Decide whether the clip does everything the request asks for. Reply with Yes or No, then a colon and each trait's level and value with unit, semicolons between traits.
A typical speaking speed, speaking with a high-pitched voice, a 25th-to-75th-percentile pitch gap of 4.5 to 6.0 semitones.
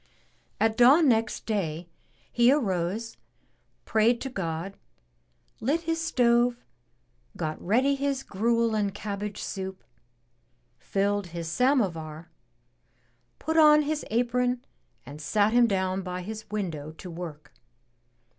No: slow, 115 wpm; high, 215 Hz; average, 5.3 semitones